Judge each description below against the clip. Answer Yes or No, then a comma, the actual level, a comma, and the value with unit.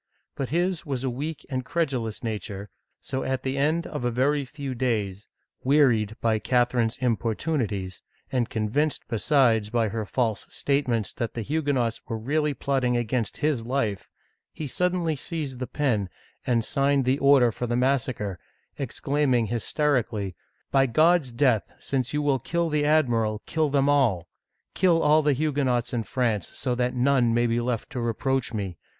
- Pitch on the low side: Yes, low, 130 Hz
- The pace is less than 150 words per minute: No, average, 165 wpm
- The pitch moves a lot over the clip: No, average, 3.9 semitones